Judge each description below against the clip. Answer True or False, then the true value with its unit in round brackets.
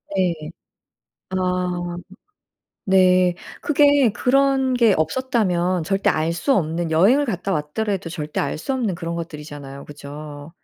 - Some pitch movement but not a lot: False (5.7 semitones)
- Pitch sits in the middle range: True (180 Hz)